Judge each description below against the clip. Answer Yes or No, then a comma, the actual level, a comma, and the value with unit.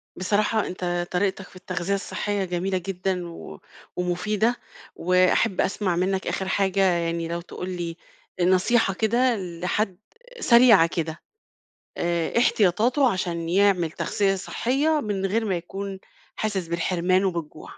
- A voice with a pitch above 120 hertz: Yes, medium, 185 Hz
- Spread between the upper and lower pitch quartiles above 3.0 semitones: No, average, 2.7 semitones